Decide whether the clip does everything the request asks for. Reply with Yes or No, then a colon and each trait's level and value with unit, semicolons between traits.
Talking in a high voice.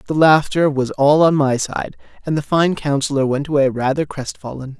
No: medium, 145 Hz